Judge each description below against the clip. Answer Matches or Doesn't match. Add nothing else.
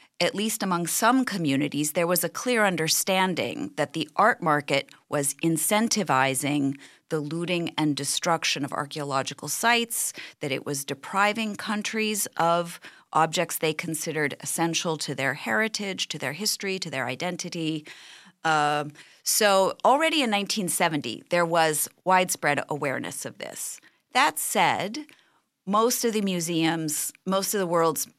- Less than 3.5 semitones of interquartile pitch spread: Doesn't match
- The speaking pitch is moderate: Matches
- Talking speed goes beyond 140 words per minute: Doesn't match